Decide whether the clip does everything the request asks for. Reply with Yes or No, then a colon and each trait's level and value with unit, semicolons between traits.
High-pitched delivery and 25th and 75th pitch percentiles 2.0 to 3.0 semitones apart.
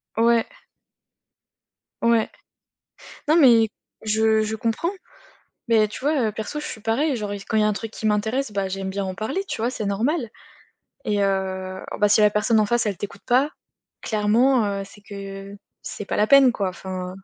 Yes: high, 215 Hz; average, 2.7 semitones